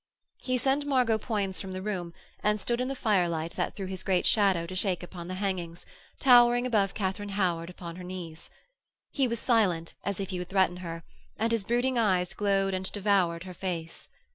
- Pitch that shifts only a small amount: No, average, 3.6 semitones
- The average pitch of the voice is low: No, high, 190 Hz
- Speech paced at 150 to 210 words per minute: Yes, average, 195 wpm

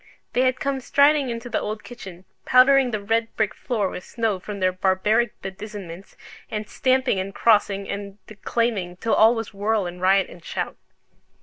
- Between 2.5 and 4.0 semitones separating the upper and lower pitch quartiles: Yes, average, 3.6 semitones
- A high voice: Yes, high, 215 Hz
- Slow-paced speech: No, average, 175 wpm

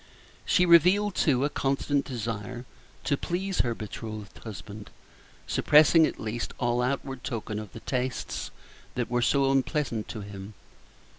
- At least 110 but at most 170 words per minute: Yes, average, 140 wpm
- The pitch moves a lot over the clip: No, average, 4.5 semitones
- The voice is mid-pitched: No, low, 125 Hz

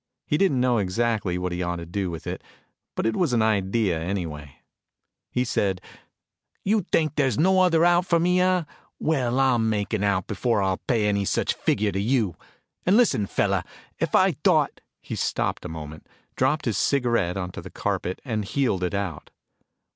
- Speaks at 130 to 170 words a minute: No, average, 185 wpm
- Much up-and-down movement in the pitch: Yes, wide, 6.6 semitones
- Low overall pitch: Yes, low, 110 Hz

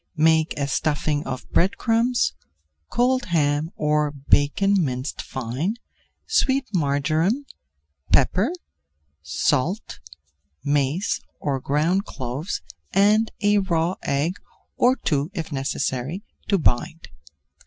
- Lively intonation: Yes, wide, 5.9 semitones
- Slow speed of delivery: Yes, slow, 100 wpm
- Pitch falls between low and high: Yes, medium, 160 Hz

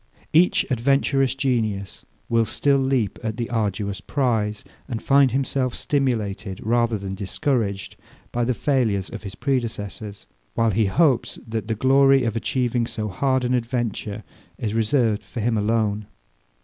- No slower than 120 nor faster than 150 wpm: Yes, average, 145 wpm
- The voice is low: Yes, low, 115 Hz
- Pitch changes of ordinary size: Yes, average, 3.7 semitones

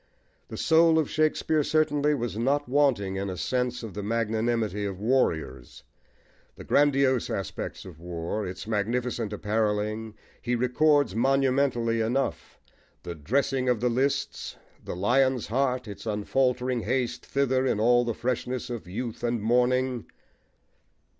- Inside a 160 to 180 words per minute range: No, slow, 135 wpm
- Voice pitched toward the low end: Yes, low, 120 Hz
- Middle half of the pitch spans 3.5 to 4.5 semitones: Yes, average, 3.8 semitones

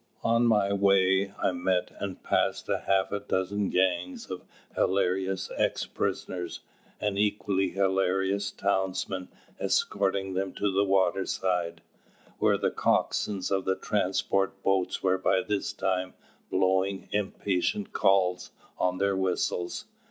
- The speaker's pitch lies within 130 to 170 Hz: No, very low, 95 Hz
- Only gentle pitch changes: Yes, narrow, 1.2 semitones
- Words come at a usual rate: No, slow, 120 wpm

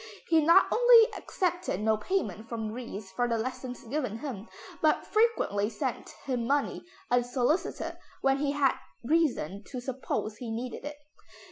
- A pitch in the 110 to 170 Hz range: No, very high, 250 Hz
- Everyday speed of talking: Yes, average, 145 wpm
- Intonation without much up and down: No, average, 5.0 semitones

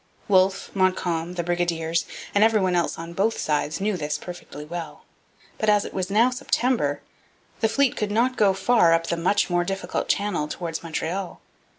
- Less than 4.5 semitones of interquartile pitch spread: Yes, average, 3.8 semitones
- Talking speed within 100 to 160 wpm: No, average, 180 wpm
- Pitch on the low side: No, medium, 185 Hz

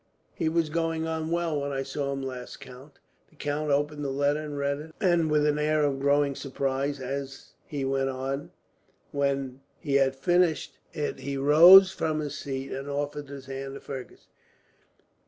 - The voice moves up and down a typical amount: No, narrow, 2.0 semitones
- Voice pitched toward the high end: No, medium, 140 Hz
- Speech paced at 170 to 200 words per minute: Yes, average, 175 wpm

